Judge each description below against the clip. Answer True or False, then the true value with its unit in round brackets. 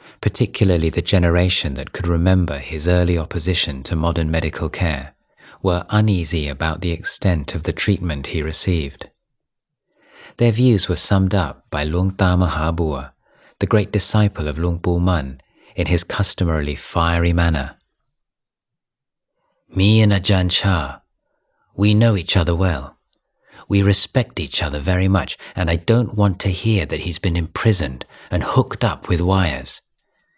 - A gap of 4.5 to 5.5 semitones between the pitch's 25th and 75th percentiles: False (3.5 semitones)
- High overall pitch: False (90 Hz)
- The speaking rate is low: False (145 wpm)